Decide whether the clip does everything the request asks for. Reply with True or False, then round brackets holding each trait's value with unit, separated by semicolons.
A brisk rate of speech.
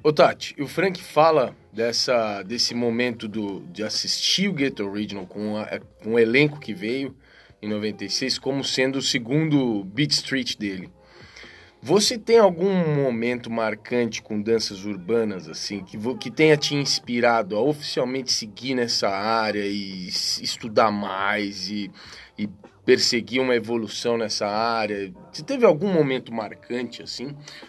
False (140 wpm)